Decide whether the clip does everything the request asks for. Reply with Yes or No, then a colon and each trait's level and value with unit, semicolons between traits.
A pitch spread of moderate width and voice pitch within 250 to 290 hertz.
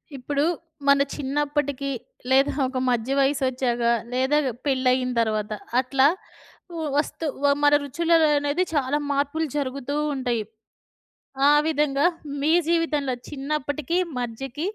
No: narrow, 2.3 semitones; very high, 275 Hz